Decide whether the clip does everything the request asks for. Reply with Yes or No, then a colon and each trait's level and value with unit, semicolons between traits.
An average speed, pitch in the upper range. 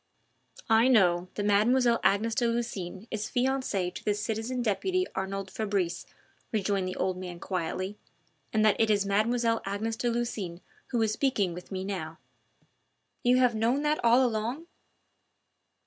Yes: average, 150 wpm; high, 215 Hz